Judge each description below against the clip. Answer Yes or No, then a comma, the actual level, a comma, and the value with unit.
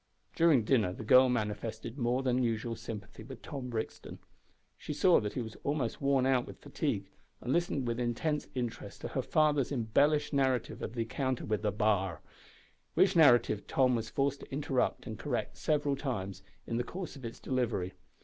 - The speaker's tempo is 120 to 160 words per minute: No, average, 180 wpm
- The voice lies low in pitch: Yes, low, 125 Hz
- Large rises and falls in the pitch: No, average, 3.8 semitones